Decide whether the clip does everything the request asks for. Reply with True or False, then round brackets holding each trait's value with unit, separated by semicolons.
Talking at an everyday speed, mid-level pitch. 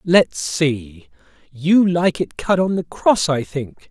True (170 wpm; 160 Hz)